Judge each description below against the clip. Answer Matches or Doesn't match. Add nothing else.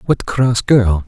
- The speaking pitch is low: Matches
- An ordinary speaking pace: Matches